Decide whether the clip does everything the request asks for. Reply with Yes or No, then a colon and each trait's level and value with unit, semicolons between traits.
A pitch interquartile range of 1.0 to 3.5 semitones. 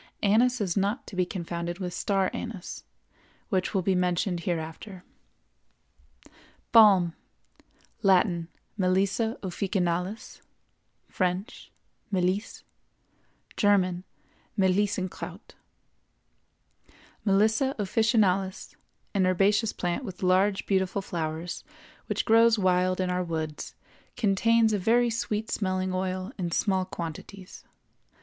Yes: narrow, 2.5 semitones